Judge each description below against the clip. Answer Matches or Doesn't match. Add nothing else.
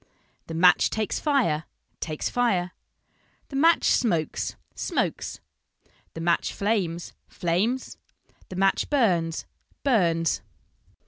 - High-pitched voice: Doesn't match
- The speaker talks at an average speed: Doesn't match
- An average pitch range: Doesn't match